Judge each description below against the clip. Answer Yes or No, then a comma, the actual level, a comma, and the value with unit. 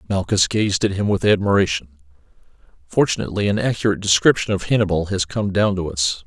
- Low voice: Yes, very low, 95 Hz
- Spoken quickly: No, average, 165 wpm